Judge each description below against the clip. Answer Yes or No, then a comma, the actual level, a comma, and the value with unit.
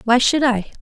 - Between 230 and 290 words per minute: No, fast, 220 wpm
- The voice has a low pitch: No, high, 245 Hz